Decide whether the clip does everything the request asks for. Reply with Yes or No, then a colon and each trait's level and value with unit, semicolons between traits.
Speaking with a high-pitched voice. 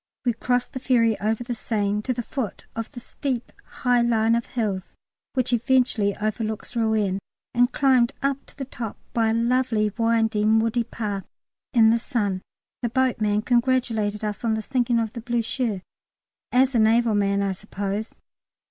Yes: high, 230 Hz